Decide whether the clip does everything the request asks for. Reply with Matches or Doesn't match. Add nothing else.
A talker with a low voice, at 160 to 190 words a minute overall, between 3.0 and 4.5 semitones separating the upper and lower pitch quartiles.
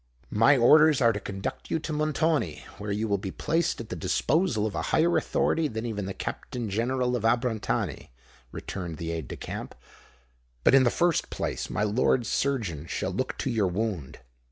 Doesn't match